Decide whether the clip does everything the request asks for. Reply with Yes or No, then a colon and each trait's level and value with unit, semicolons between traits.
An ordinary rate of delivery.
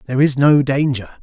Yes: average, 195 wpm